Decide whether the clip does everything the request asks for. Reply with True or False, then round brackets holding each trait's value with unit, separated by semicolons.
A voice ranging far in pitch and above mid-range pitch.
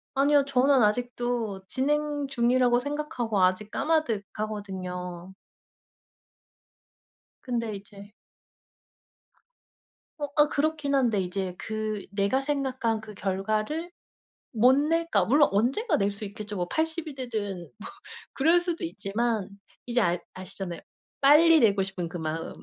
True (6.1 semitones; 230 Hz)